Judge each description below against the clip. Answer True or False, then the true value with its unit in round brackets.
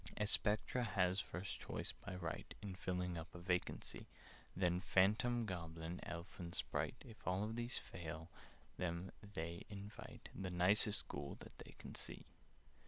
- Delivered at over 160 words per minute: False (150 wpm)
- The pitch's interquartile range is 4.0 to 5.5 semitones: False (3.1 semitones)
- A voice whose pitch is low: True (90 Hz)